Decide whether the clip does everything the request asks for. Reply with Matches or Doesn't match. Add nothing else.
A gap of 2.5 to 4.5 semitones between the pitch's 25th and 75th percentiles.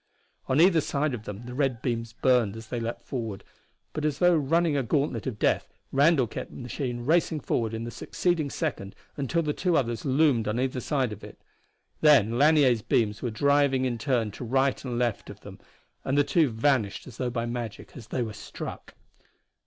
Matches